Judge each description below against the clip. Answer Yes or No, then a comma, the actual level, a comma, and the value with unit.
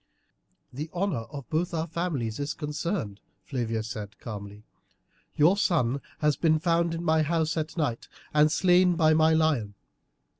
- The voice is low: No, medium, 155 Hz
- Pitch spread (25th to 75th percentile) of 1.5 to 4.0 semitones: No, wide, 5.5 semitones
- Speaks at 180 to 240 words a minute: No, average, 150 wpm